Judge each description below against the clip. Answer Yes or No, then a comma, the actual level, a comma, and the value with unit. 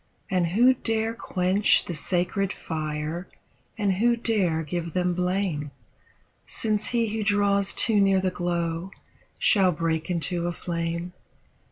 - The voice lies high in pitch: No, medium, 180 Hz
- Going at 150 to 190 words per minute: No, slow, 135 wpm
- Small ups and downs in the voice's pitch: No, average, 3.3 semitones